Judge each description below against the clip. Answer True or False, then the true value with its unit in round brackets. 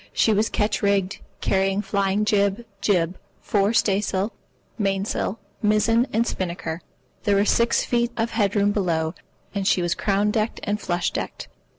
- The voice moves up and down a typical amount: False (1.8 semitones)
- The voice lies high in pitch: True (200 Hz)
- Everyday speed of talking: True (160 wpm)